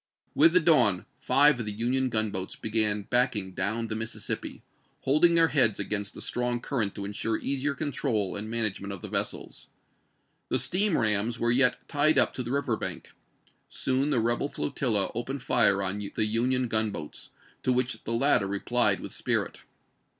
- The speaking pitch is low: Yes, low, 115 Hz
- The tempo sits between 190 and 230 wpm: No, average, 170 wpm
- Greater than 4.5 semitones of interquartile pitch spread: No, average, 4.2 semitones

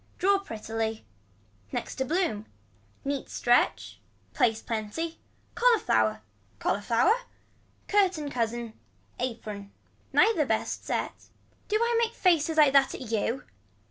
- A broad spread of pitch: Yes, wide, 8.0 semitones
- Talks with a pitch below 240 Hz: No, very high, 255 Hz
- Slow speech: Yes, slow, 110 wpm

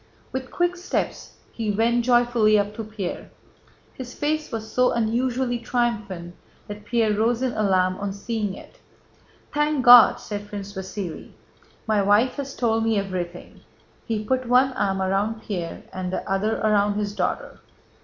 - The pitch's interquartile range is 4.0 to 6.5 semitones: No, average, 3.3 semitones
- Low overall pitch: No, high, 220 Hz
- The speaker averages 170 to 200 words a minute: No, average, 155 wpm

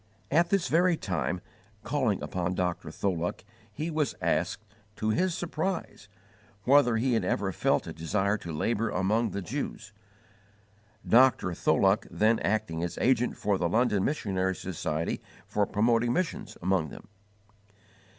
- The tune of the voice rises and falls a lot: Yes, wide, 5.8 semitones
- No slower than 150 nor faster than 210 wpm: No, average, 140 wpm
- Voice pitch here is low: Yes, low, 105 Hz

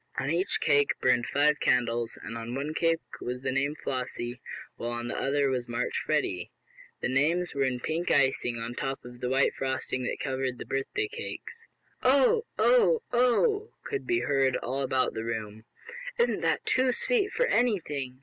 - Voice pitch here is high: No, low, 135 Hz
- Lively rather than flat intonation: Yes, wide, 6.3 semitones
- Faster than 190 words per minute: No, average, 175 wpm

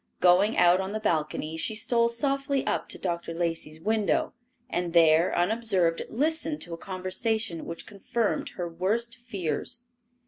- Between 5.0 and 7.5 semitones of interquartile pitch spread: Yes, wide, 5.4 semitones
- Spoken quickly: No, average, 145 wpm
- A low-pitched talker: No, high, 190 Hz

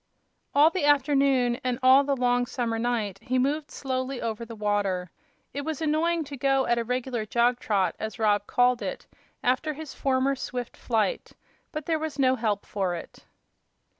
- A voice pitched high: Yes, very high, 255 Hz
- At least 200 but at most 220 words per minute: No, average, 175 wpm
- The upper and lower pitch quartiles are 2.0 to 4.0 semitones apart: Yes, average, 3.5 semitones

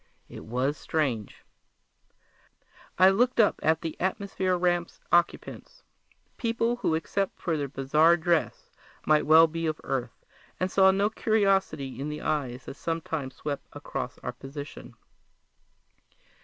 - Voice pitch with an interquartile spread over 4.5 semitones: Yes, average, 5.0 semitones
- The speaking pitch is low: No, medium, 160 Hz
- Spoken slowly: Yes, slow, 130 wpm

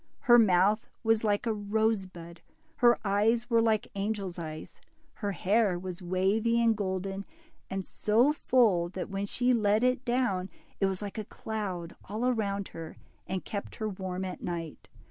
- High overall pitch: Yes, high, 205 Hz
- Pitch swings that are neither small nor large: Yes, average, 3.2 semitones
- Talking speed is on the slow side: No, average, 165 wpm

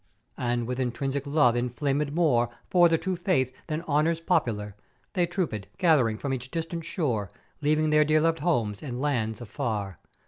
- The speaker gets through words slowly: No, average, 165 wpm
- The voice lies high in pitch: No, medium, 140 Hz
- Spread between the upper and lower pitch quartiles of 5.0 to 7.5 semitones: Yes, average, 5.3 semitones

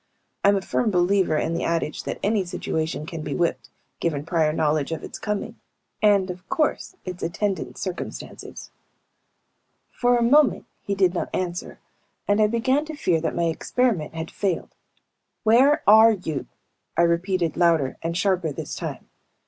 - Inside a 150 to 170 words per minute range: Yes, average, 160 wpm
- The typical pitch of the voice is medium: Yes, medium, 180 Hz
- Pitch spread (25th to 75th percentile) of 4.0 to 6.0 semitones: Yes, average, 4.3 semitones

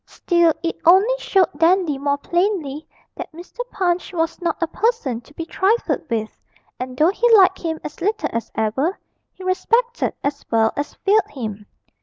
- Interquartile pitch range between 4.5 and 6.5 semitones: Yes, average, 5.2 semitones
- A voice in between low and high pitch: No, very high, 335 Hz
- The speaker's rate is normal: Yes, average, 170 wpm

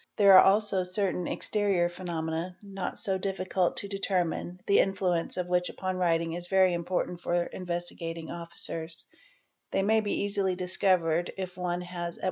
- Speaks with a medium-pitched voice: Yes, medium, 180 Hz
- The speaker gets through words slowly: No, average, 155 wpm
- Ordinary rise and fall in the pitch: No, narrow, 1.9 semitones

